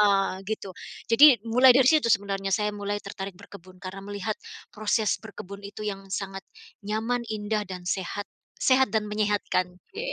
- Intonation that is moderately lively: No, narrow, 2.0 semitones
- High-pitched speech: Yes, high, 205 Hz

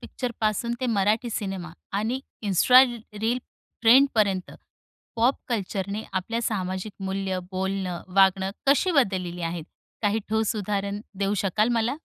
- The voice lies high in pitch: Yes, high, 205 Hz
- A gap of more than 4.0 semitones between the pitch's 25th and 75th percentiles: No, average, 3.3 semitones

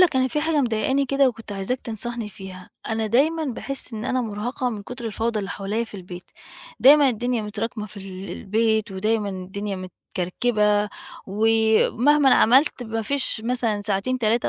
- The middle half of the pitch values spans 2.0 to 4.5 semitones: Yes, average, 3.5 semitones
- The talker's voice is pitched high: Yes, high, 225 Hz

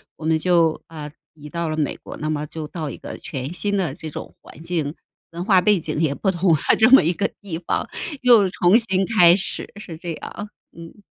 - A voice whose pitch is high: No, medium, 170 Hz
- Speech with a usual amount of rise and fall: Yes, average, 3.6 semitones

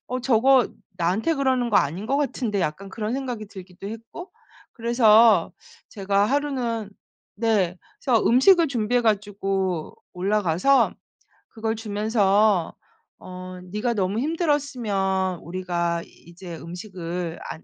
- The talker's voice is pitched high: Yes, high, 210 Hz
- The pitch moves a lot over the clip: No, average, 4.7 semitones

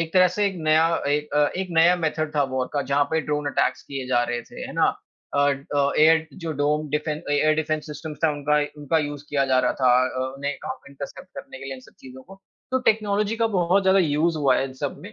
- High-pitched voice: No, medium, 150 Hz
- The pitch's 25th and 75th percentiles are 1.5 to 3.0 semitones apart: Yes, average, 2.7 semitones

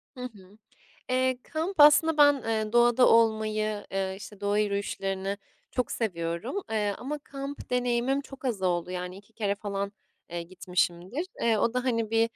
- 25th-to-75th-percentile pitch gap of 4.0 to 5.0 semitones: Yes, average, 4.3 semitones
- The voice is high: Yes, high, 220 Hz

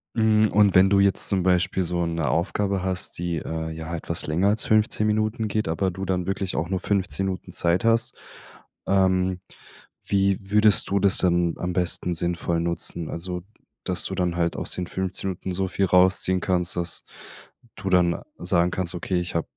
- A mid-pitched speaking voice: No, very low, 90 Hz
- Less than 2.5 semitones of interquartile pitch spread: Yes, narrow, 2.1 semitones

